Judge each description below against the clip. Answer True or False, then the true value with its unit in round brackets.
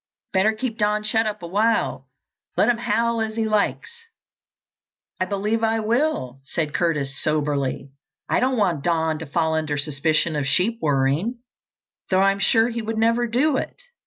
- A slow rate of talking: False (160 wpm)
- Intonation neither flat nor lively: False (6.6 semitones)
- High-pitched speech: True (200 Hz)